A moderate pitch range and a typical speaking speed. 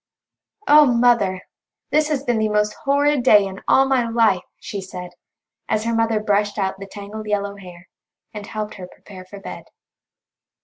Yes: average, 3.1 semitones; average, 170 wpm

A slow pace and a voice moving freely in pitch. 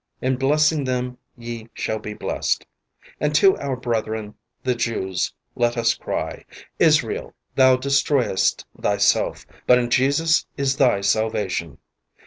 No: slow, 125 wpm; average, 3.7 semitones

